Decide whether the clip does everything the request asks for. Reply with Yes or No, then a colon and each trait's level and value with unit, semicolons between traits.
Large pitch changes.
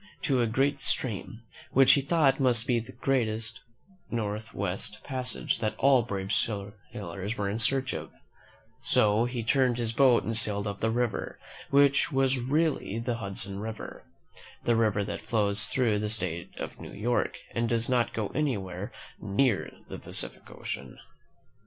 No: average, 3.9 semitones